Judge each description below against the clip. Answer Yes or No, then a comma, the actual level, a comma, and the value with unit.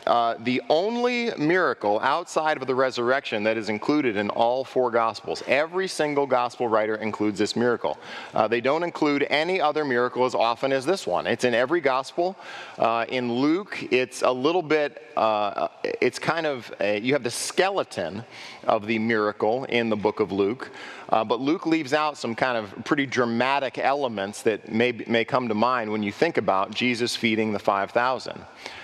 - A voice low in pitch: Yes, low, 125 Hz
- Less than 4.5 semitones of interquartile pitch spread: No, average, 5.1 semitones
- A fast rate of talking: No, average, 180 wpm